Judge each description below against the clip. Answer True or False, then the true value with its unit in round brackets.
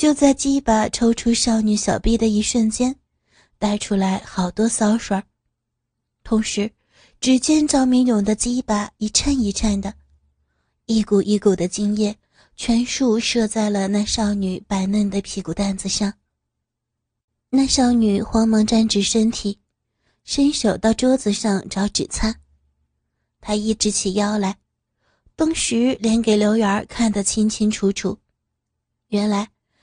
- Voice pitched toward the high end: True (210 Hz)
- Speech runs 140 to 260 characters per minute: True (195 characters per minute)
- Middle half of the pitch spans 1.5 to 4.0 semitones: True (2.6 semitones)